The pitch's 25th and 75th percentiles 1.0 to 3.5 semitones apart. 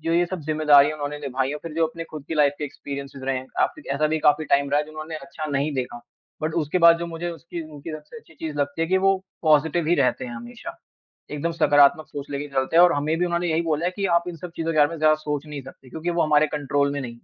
Yes: narrow, 2.5 semitones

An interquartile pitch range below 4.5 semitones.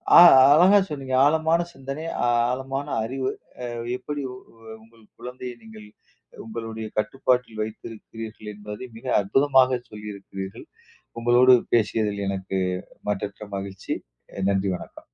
Yes: average, 4.0 semitones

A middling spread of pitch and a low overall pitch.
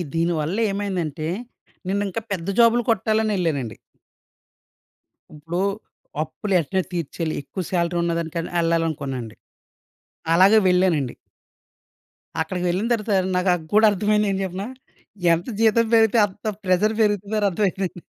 No: average, 3.7 semitones; medium, 185 Hz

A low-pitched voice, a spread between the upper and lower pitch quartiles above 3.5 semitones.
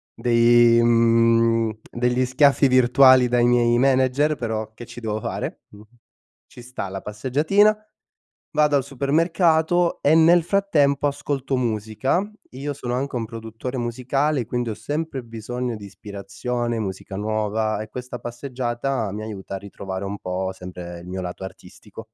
Yes: low, 120 Hz; average, 4.0 semitones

